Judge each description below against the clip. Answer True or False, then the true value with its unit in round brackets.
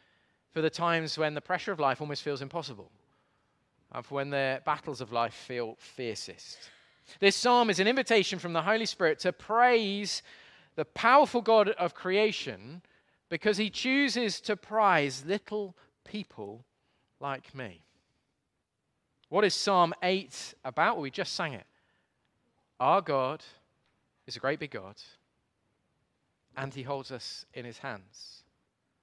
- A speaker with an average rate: True (145 wpm)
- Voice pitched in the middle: True (170 Hz)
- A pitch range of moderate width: False (7.2 semitones)